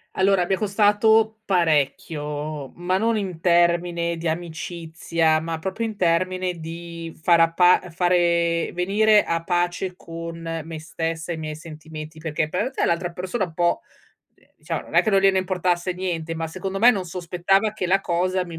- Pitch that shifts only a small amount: Yes, narrow, 2.3 semitones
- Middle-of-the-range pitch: Yes, medium, 175 Hz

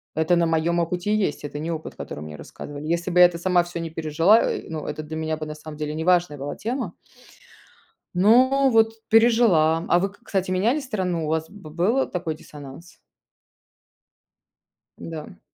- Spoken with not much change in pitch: No, average, 3.9 semitones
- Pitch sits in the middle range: Yes, medium, 170 Hz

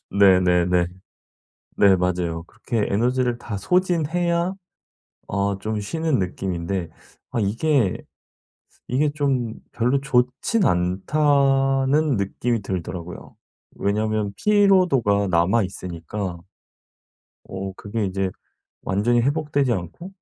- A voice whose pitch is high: No, low, 110 Hz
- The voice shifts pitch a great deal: Yes, wide, 6.6 semitones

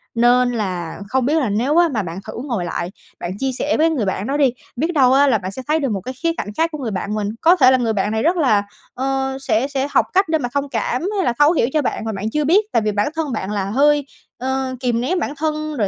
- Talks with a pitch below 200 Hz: No, very high, 260 Hz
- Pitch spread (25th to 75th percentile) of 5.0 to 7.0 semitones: Yes, wide, 5.4 semitones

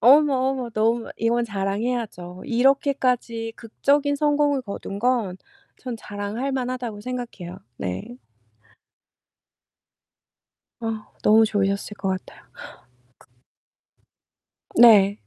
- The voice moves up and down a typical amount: Yes, average, 4.0 semitones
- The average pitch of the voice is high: Yes, high, 230 Hz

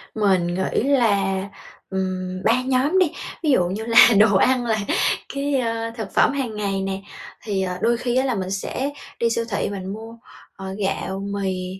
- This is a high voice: Yes, high, 210 Hz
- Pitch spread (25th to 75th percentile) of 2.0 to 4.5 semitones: Yes, average, 4.0 semitones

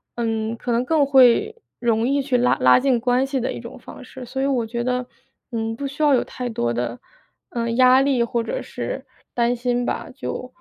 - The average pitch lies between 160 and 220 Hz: No, high, 245 Hz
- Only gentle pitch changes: Yes, narrow, 2.3 semitones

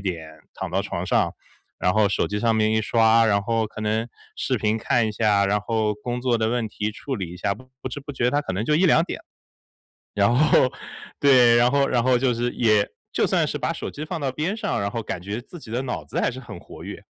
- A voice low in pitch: Yes, low, 115 Hz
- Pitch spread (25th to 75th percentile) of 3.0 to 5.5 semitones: Yes, average, 3.4 semitones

